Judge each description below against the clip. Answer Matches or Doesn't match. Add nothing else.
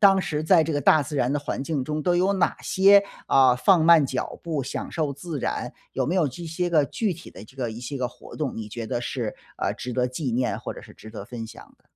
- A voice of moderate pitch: Matches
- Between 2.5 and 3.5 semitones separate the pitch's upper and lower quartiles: Doesn't match